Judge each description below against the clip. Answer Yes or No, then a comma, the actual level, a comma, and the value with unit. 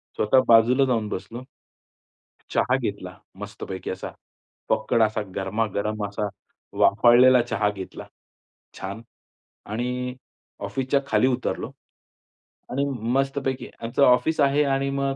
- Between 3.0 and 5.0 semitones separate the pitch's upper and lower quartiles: Yes, average, 3.7 semitones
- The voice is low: Yes, low, 120 Hz